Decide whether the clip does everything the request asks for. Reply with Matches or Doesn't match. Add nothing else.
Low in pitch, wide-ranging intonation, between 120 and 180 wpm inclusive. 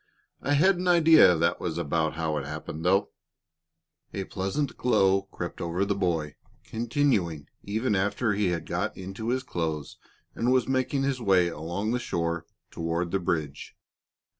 Matches